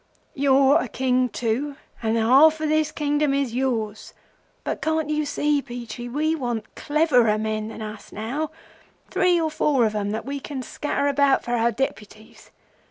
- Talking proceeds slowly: No, average, 165 wpm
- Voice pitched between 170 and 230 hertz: No, very high, 265 Hz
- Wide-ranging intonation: No, average, 4.7 semitones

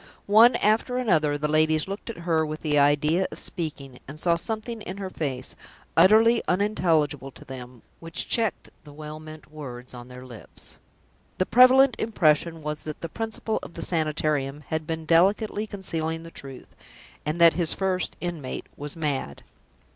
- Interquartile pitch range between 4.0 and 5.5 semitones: Yes, average, 4.5 semitones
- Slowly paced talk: No, average, 165 wpm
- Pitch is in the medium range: Yes, medium, 160 Hz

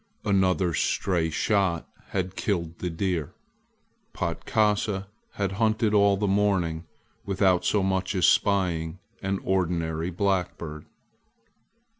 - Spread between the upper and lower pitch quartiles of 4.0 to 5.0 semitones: No, average, 2.8 semitones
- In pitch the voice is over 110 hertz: No, very low, 95 Hz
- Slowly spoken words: Yes, slow, 105 wpm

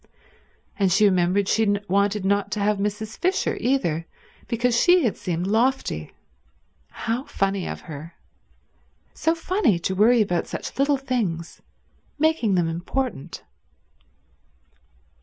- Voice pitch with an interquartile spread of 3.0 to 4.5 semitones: No, wide, 5.4 semitones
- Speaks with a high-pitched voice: Yes, high, 205 Hz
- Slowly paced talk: Yes, slow, 125 wpm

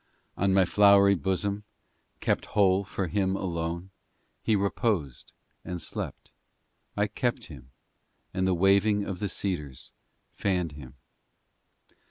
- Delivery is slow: Yes, slow, 125 wpm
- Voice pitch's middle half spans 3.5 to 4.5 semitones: No, narrow, 2.5 semitones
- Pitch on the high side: No, very low, 95 Hz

